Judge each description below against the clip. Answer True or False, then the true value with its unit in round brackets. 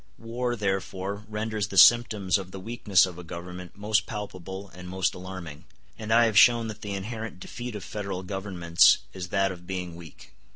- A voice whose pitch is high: False (95 Hz)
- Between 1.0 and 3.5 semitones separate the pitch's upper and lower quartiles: True (3.0 semitones)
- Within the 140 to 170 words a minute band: False (180 wpm)